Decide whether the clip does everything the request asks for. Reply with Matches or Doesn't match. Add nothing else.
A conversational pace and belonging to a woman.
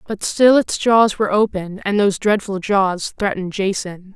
Matches